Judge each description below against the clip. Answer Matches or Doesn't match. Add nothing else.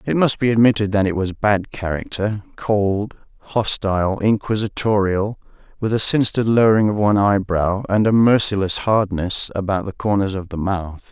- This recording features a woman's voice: Doesn't match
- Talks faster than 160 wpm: Doesn't match